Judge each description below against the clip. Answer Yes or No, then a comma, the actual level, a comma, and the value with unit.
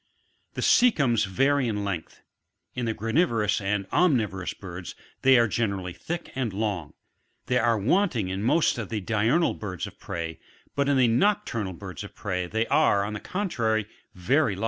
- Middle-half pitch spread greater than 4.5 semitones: Yes, average, 5.0 semitones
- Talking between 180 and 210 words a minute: Yes, average, 185 wpm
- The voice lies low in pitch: Yes, low, 110 Hz